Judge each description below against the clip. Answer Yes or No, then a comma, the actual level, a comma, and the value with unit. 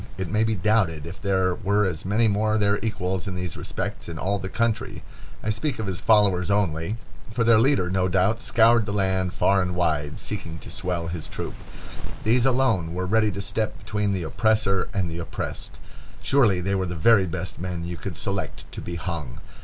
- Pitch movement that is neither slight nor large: Yes, average, 3.4 semitones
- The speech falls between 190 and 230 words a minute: Yes, average, 195 wpm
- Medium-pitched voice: No, very low, 95 Hz